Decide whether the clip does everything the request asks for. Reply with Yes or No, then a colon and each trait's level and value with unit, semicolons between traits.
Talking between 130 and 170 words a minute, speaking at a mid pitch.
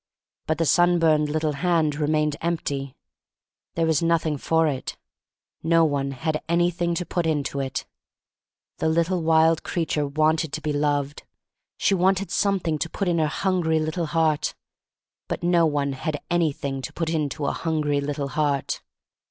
Yes: average, 160 wpm; medium, 160 Hz